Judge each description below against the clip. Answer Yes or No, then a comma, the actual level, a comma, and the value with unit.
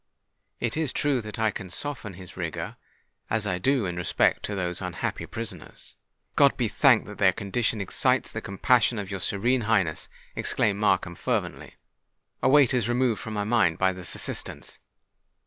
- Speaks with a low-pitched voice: Yes, low, 105 Hz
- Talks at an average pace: Yes, average, 170 wpm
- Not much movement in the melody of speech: No, average, 4.4 semitones